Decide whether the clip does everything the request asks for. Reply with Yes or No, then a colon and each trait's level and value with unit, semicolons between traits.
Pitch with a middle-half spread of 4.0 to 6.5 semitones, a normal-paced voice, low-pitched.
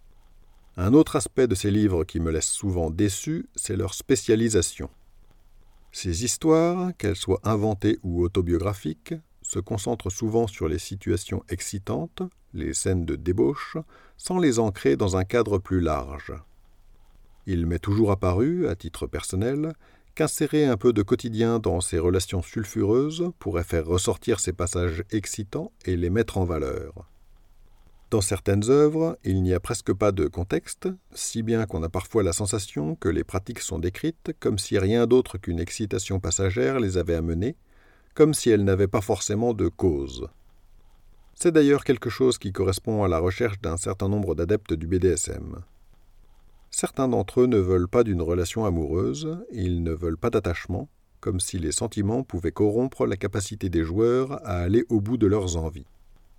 Yes: average, 4.8 semitones; average, 165 wpm; low, 100 Hz